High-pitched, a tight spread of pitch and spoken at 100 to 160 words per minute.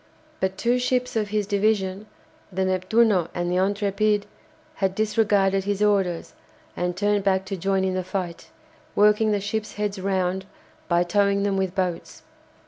Yes: high, 195 Hz; narrow, 1.8 semitones; average, 155 wpm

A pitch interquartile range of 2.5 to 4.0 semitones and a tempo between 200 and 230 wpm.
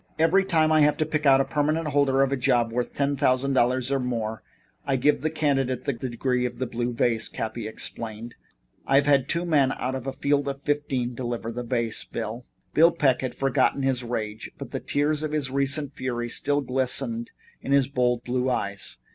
Yes: average, 2.9 semitones; fast, 205 wpm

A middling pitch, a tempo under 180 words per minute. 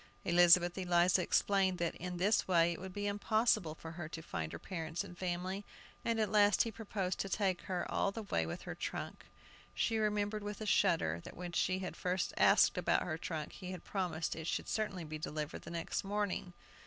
No: medium, 180 Hz; fast, 205 wpm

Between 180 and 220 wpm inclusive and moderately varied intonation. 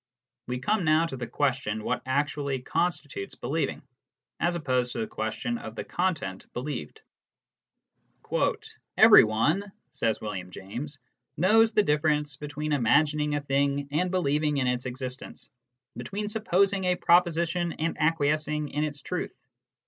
No: slow, 135 wpm; average, 4.8 semitones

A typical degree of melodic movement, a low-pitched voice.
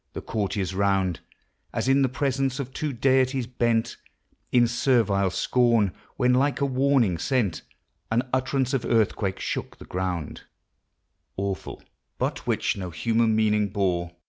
Yes: average, 4.9 semitones; low, 115 Hz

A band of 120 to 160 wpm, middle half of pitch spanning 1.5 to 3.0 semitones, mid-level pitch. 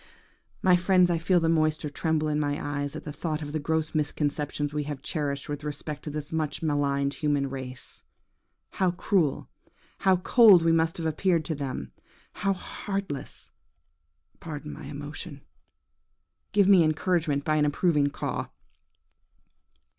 Yes: average, 145 wpm; narrow, 2.6 semitones; medium, 155 Hz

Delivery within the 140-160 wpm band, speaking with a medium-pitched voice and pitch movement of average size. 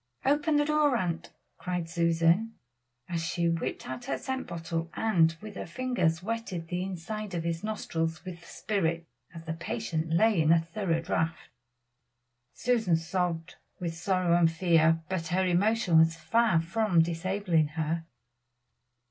Yes: average, 150 wpm; medium, 170 Hz; average, 3.9 semitones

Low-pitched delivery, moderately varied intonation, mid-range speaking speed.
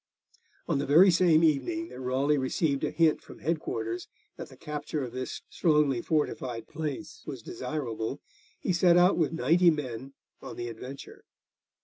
No: medium, 145 Hz; average, 4.3 semitones; average, 160 wpm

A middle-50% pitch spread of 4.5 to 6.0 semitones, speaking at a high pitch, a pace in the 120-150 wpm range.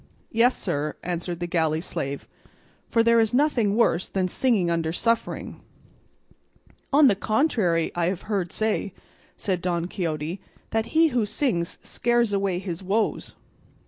Yes: average, 5.0 semitones; high, 195 Hz; average, 145 wpm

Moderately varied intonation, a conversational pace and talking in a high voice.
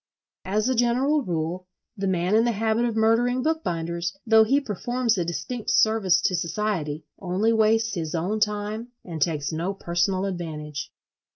Yes: average, 4.7 semitones; average, 160 wpm; high, 205 Hz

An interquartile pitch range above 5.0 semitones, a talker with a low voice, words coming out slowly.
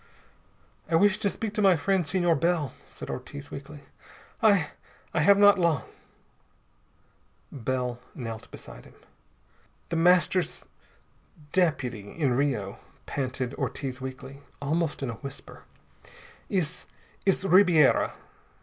No: wide, 5.6 semitones; medium, 150 Hz; slow, 115 wpm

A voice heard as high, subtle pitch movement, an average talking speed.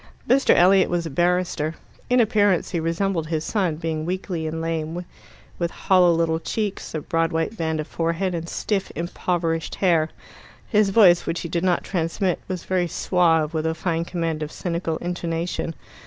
No: medium, 170 Hz; narrow, 2.0 semitones; average, 170 wpm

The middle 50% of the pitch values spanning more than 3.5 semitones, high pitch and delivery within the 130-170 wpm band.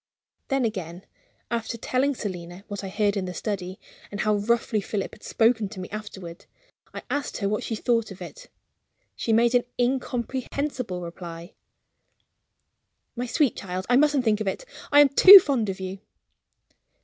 Yes: average, 4.6 semitones; high, 215 Hz; average, 165 wpm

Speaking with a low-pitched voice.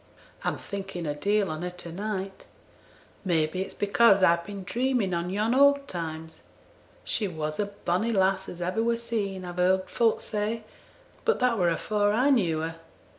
No: high, 195 Hz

